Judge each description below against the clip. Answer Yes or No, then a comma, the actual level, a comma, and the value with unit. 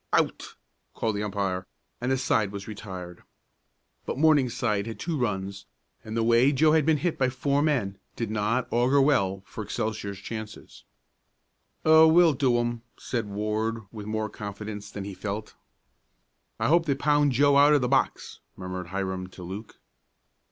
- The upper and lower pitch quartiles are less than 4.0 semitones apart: No, average, 5.3 semitones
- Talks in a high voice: No, low, 110 Hz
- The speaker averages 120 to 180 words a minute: Yes, average, 165 wpm